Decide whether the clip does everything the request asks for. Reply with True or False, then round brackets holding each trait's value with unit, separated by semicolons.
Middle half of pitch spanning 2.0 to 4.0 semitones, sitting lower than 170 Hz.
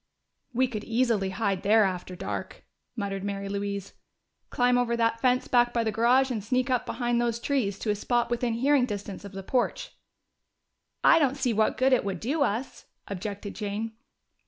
False (3.7 semitones; 230 Hz)